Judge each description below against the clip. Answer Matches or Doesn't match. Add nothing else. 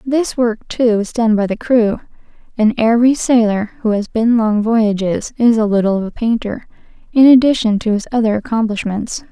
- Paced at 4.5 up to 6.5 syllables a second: Matches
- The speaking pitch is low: Doesn't match